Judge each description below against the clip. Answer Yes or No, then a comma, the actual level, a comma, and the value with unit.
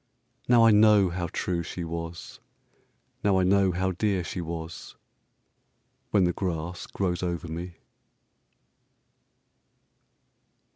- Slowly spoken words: Yes, slow, 100 wpm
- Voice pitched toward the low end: Yes, very low, 90 Hz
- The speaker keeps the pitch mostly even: Yes, narrow, 2.2 semitones